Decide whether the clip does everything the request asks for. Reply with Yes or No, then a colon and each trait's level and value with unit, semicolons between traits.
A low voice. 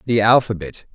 Yes: low, 110 Hz